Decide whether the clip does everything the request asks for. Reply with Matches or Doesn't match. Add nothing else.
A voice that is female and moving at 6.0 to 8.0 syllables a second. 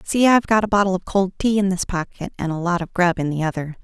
Matches